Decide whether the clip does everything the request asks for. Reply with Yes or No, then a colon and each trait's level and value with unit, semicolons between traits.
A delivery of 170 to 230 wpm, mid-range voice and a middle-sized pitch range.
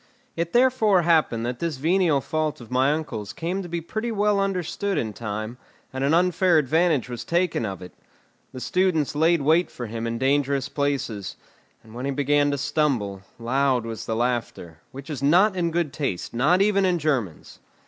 No: average, 185 wpm; medium, 145 Hz; wide, 6.1 semitones